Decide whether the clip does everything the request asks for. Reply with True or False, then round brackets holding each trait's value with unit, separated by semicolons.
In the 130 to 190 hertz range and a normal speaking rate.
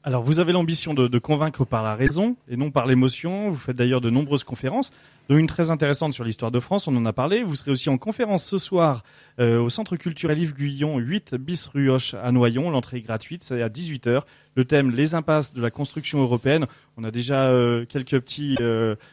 False (140 Hz; 225 wpm)